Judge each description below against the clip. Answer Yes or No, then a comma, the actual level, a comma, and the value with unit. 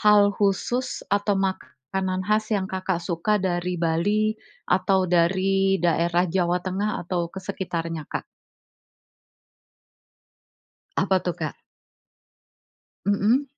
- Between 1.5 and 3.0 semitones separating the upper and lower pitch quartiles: Yes, average, 2.7 semitones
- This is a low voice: No, high, 190 Hz